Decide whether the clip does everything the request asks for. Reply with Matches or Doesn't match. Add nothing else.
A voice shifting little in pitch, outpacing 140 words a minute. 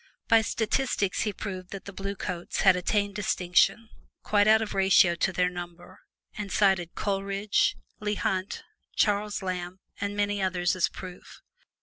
Matches